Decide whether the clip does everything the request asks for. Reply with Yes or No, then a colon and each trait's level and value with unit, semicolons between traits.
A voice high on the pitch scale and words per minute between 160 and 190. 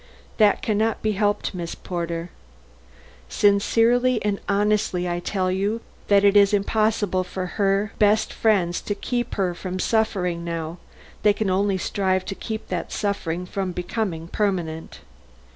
No: high, 200 Hz; average, 145 wpm